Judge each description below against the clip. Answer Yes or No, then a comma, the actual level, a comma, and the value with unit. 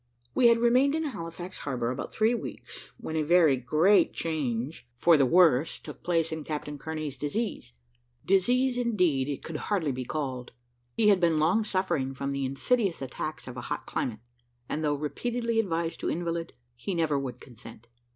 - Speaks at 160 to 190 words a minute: Yes, average, 175 wpm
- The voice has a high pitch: No, medium, 160 Hz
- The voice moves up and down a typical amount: No, wide, 6.0 semitones